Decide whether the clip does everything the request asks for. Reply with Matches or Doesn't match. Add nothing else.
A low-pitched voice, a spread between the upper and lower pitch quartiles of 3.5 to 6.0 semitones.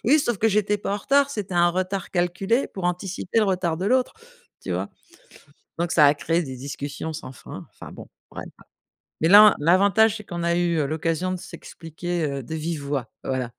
Doesn't match